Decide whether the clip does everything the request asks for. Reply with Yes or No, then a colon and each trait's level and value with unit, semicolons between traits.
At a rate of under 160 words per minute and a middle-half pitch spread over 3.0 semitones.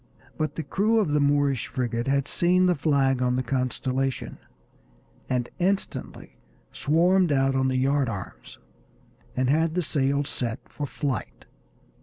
Yes: average, 145 wpm; average, 3.5 semitones